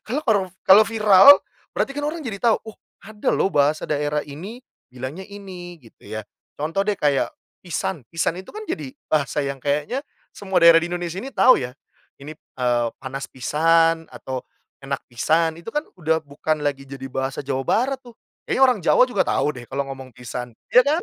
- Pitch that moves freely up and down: Yes, wide, 6.7 semitones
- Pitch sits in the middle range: Yes, medium, 165 Hz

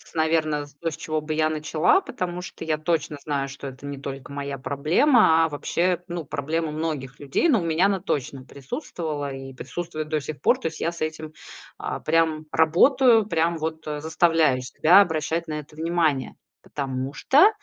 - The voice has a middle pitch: Yes, medium, 155 Hz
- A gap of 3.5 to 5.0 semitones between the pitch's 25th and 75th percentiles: No, average, 2.7 semitones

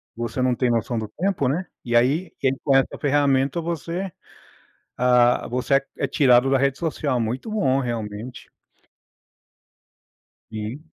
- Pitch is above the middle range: No, low, 130 Hz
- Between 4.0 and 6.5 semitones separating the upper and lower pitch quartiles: No, average, 3.3 semitones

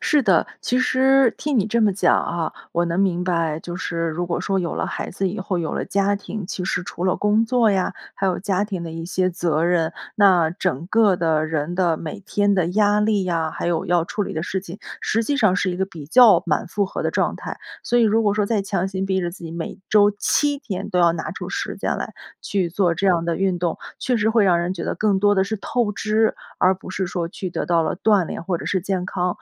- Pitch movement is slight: No, average, 3.2 semitones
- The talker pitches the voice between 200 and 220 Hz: No, high, 190 Hz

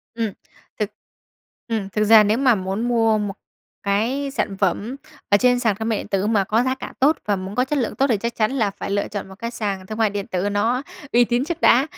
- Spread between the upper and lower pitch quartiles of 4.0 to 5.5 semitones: No, average, 3.3 semitones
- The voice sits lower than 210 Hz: No, high, 220 Hz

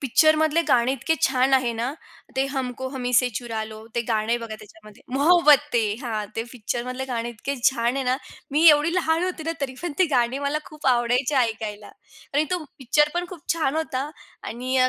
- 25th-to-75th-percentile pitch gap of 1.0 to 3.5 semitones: No, average, 4.1 semitones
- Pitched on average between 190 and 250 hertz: No, very high, 260 Hz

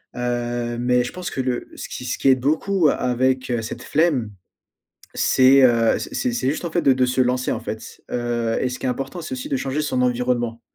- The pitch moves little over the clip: Yes, narrow, 2.2 semitones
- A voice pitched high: No, low, 125 Hz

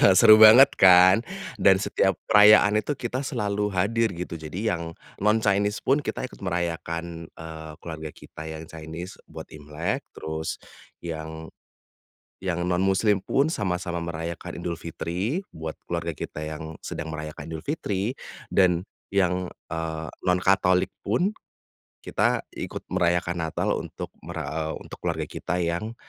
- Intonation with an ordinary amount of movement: Yes, average, 4.0 semitones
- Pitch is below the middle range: Yes, very low, 90 Hz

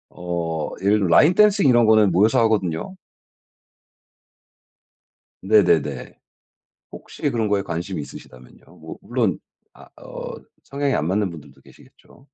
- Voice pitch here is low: Yes, low, 100 Hz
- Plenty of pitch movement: No, average, 4.9 semitones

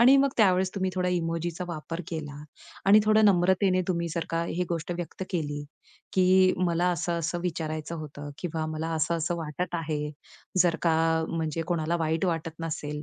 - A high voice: No, medium, 170 Hz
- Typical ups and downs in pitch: No, narrow, 2.2 semitones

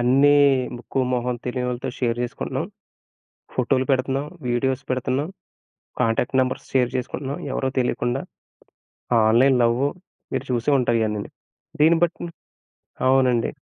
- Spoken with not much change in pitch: Yes, narrow, 1.7 semitones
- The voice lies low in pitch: Yes, low, 125 Hz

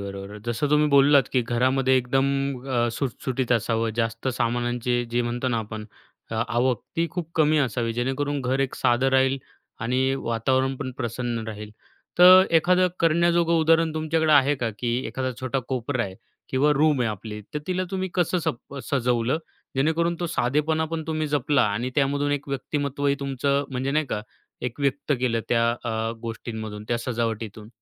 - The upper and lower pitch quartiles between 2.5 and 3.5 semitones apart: No, average, 3.9 semitones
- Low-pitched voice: Yes, low, 130 Hz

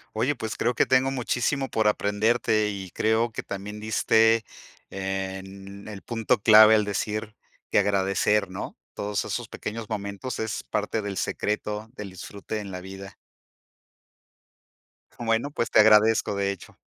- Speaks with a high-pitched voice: No, low, 105 Hz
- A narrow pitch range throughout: Yes, narrow, 2.1 semitones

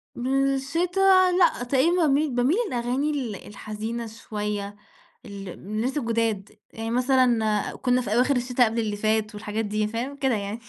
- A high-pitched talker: Yes, high, 240 Hz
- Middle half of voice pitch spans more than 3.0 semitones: Yes, average, 4.1 semitones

